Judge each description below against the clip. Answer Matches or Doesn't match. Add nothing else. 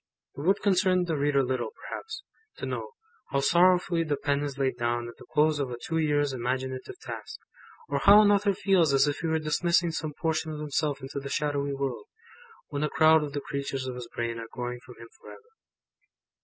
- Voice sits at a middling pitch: Matches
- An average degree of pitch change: Matches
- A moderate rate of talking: Doesn't match